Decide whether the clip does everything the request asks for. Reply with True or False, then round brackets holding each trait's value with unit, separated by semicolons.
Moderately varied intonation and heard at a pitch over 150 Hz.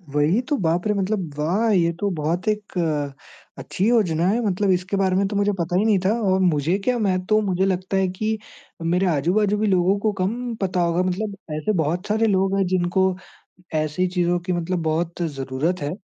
True (3.0 semitones; 185 Hz)